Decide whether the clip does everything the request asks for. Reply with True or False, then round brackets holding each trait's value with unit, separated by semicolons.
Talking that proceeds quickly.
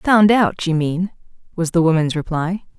False (170 wpm)